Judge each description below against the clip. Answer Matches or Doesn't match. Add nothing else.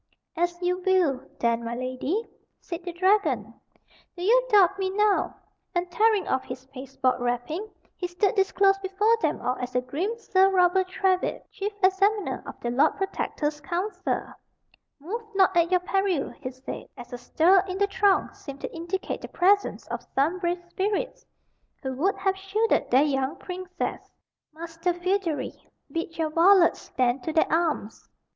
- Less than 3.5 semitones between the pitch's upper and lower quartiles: Doesn't match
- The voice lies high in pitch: Matches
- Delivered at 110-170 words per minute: Matches